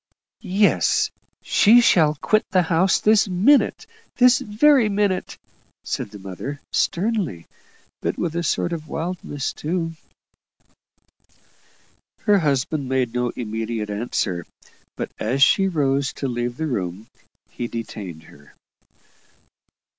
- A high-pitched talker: No, medium, 150 Hz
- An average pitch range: No, wide, 8.4 semitones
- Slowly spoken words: Yes, slow, 115 wpm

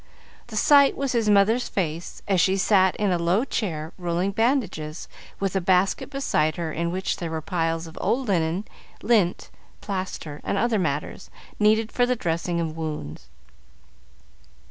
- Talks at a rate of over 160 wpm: No, average, 155 wpm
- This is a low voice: No, medium, 185 Hz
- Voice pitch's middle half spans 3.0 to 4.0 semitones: No, average, 4.6 semitones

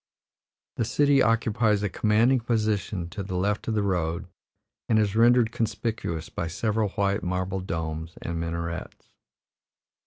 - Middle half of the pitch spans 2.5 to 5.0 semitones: Yes, average, 4.4 semitones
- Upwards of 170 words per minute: No, slow, 135 wpm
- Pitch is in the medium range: No, low, 105 Hz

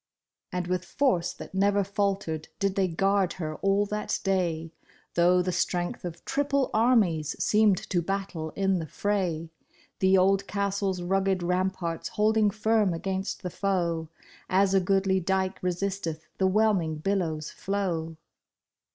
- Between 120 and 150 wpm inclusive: Yes, average, 140 wpm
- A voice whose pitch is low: No, high, 190 Hz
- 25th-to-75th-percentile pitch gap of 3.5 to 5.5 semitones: No, narrow, 2.4 semitones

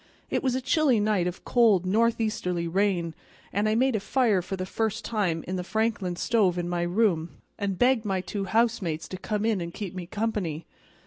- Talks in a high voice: Yes, high, 200 Hz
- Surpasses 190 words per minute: Yes, average, 200 wpm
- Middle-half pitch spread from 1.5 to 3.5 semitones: No, average, 3.9 semitones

